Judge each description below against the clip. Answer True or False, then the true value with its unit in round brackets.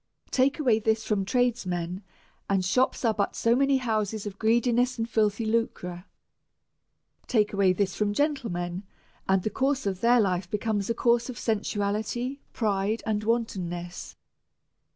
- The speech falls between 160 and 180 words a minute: False (145 wpm)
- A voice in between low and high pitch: False (215 Hz)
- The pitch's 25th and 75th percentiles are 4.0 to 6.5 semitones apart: False (3.5 semitones)